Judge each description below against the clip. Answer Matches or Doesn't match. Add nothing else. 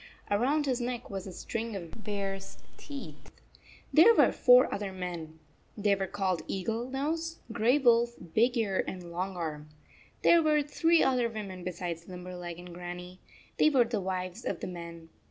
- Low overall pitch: Doesn't match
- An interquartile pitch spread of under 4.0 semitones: Doesn't match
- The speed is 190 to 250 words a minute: Doesn't match